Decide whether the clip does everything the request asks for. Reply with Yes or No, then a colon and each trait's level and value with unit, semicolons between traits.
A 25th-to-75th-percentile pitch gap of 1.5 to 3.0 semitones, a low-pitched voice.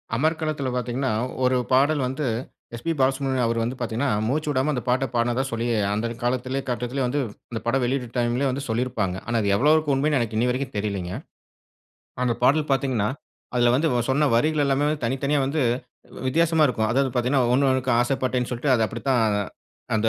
Yes: average, 2.7 semitones; low, 130 Hz